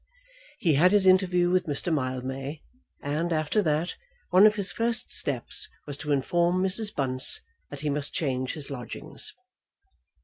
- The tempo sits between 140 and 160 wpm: Yes, average, 150 wpm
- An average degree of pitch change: Yes, average, 4.7 semitones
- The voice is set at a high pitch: No, medium, 155 Hz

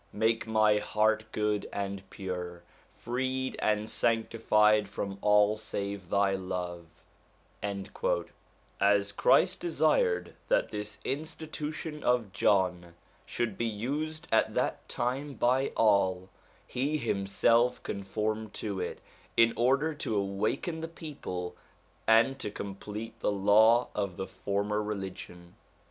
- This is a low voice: Yes, low, 105 Hz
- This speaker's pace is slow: Yes, slow, 115 wpm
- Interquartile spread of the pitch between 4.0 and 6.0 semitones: No, average, 3.6 semitones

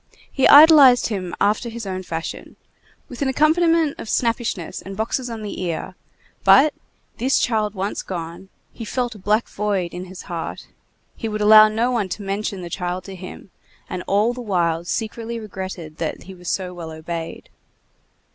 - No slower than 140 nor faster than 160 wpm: No, average, 175 wpm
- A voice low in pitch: No, high, 205 Hz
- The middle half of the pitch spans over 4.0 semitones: Yes, average, 4.4 semitones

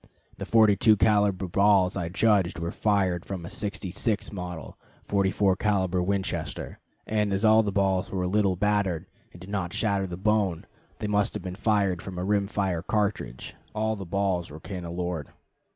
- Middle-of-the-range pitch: No, very low, 95 Hz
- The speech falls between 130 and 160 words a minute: No, average, 170 wpm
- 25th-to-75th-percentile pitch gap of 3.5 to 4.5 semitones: No, narrow, 2.5 semitones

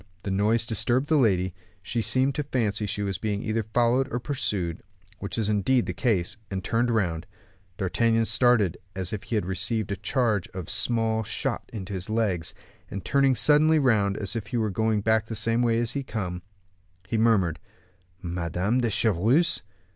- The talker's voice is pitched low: Yes, low, 110 Hz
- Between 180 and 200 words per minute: Yes, average, 185 wpm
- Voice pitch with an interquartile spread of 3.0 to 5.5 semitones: Yes, average, 3.6 semitones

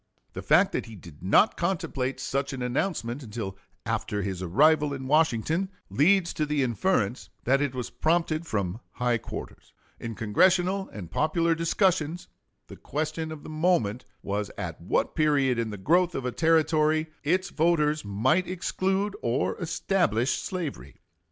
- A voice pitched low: No, medium, 150 Hz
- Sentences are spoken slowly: No, average, 150 wpm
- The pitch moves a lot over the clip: Yes, wide, 6.3 semitones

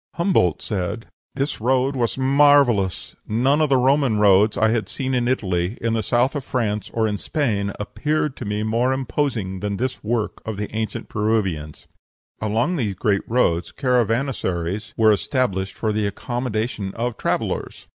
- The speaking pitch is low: Yes, low, 110 Hz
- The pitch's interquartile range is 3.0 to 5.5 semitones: Yes, average, 4.0 semitones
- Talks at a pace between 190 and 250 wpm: No, average, 160 wpm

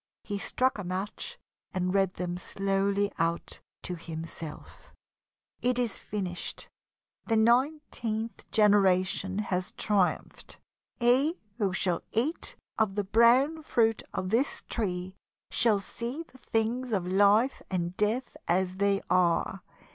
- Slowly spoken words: Yes, slow, 125 wpm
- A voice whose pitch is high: Yes, high, 205 Hz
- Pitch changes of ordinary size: Yes, average, 4.2 semitones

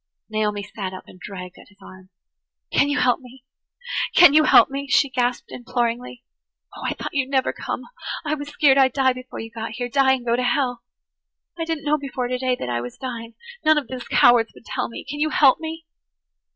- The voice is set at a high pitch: Yes, very high, 255 Hz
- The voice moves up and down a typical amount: Yes, average, 3.4 semitones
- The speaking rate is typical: No, fast, 210 wpm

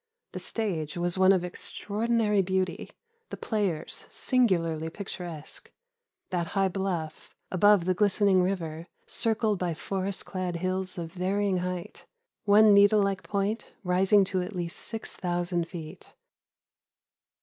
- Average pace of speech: No, slow, 125 wpm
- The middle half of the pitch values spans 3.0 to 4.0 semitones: No, narrow, 2.5 semitones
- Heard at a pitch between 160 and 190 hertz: Yes, medium, 185 Hz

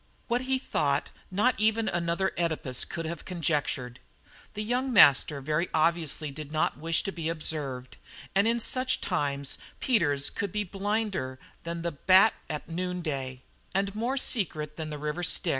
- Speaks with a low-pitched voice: No, medium, 170 Hz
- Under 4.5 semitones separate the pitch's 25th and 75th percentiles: No, average, 5.3 semitones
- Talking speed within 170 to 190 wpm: No, average, 160 wpm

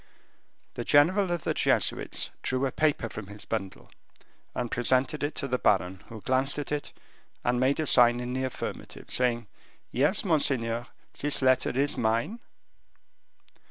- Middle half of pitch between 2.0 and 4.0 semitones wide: Yes, average, 3.6 semitones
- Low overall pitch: Yes, low, 130 Hz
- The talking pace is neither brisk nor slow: Yes, average, 155 wpm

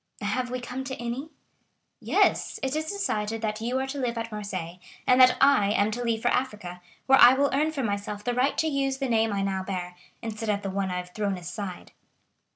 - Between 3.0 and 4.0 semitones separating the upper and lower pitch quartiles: No, average, 4.6 semitones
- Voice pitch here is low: No, high, 230 Hz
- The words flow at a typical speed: No, fast, 225 wpm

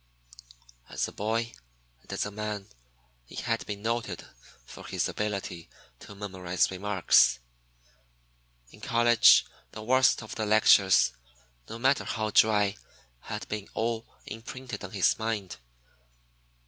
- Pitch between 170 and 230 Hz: No, low, 105 Hz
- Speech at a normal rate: No, slow, 125 wpm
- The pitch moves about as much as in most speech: No, narrow, 2.3 semitones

